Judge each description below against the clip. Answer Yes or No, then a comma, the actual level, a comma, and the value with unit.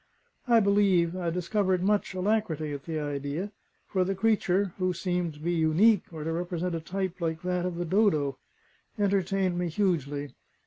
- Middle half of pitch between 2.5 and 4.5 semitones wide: Yes, average, 3.2 semitones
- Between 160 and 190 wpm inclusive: Yes, average, 170 wpm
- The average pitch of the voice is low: No, medium, 180 Hz